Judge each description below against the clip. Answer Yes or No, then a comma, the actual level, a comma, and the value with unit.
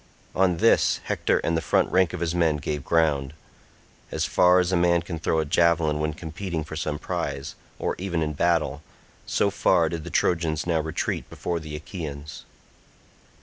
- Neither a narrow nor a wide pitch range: No, narrow, 2.2 semitones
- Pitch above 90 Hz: No, very low, 80 Hz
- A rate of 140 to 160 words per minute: No, average, 175 wpm